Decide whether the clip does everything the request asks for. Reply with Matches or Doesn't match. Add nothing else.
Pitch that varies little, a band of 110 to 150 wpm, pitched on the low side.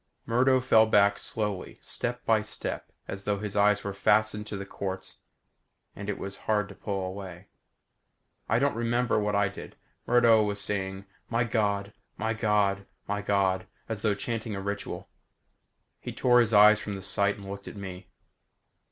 Doesn't match